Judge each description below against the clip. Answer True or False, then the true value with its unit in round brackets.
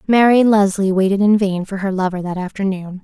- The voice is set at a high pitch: True (195 Hz)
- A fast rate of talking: False (195 wpm)